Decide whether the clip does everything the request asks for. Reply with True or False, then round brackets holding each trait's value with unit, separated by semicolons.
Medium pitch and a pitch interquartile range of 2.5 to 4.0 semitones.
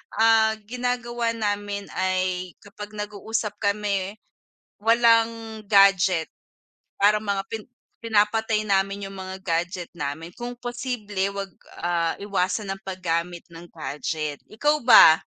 False (205 Hz; 3.3 semitones)